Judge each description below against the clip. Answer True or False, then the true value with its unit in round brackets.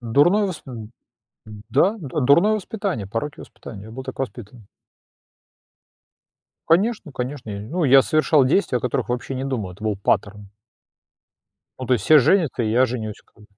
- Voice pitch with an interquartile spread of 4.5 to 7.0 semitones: True (5.6 semitones)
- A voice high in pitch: False (130 Hz)